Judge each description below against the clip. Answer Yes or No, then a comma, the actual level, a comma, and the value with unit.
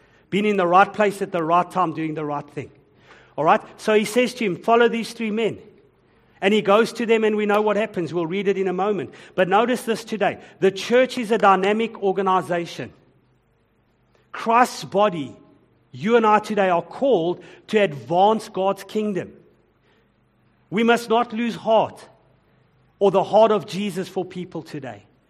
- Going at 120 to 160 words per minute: No, average, 180 wpm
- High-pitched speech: Yes, high, 195 Hz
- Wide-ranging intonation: No, average, 4.0 semitones